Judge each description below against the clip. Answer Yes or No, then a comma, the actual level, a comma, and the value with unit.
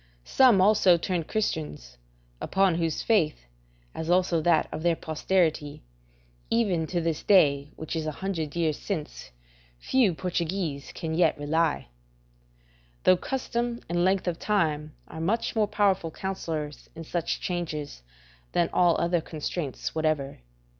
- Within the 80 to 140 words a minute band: Yes, slow, 135 wpm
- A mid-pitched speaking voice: Yes, medium, 170 Hz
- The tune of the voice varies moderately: Yes, average, 3.4 semitones